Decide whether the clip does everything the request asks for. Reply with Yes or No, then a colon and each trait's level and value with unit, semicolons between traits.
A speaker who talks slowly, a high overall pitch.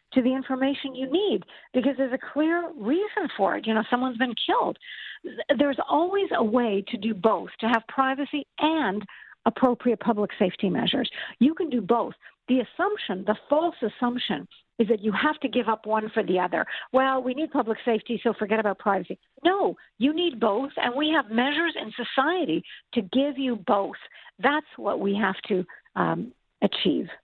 No: average, 180 wpm; very high, 250 Hz